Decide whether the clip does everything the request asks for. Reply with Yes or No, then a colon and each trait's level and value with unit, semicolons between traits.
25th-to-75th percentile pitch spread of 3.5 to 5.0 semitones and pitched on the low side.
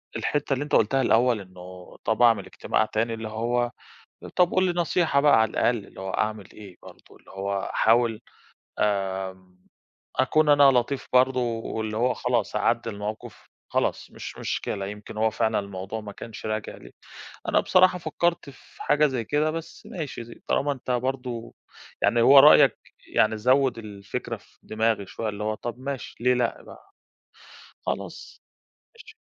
Yes: average, 4.1 semitones; low, 115 Hz